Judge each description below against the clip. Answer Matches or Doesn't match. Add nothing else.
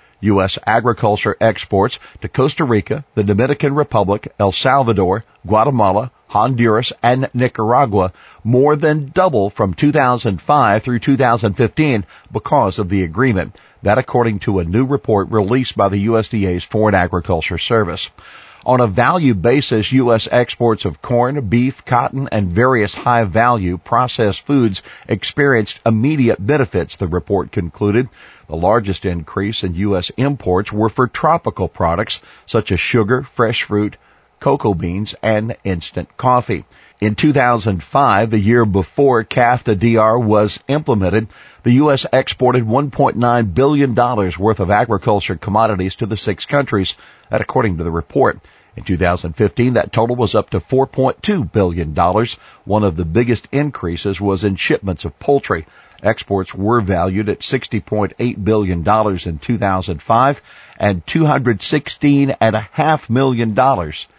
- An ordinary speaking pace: Doesn't match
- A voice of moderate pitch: Doesn't match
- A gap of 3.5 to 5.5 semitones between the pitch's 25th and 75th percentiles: Matches